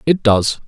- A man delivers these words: Yes, male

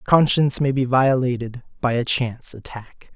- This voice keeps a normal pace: Yes, average, 150 wpm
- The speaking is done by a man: Yes, male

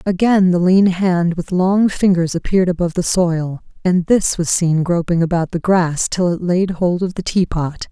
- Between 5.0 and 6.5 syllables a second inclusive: No, 4.6 syllables/s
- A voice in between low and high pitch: Yes, medium, 175 Hz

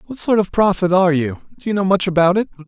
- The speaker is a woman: No, male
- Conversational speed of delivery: No, fast, 270 wpm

